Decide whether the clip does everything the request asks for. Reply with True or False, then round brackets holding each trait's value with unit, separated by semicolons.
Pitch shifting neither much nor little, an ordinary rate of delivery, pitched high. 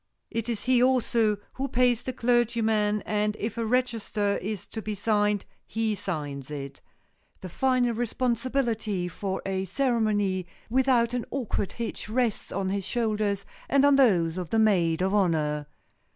True (3.8 semitones; 150 wpm; 215 Hz)